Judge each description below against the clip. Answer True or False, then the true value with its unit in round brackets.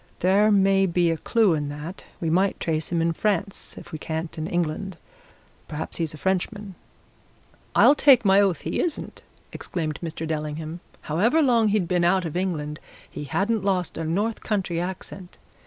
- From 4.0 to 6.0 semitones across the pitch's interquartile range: False (3.6 semitones)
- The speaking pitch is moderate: True (180 Hz)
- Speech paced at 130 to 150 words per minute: False (175 wpm)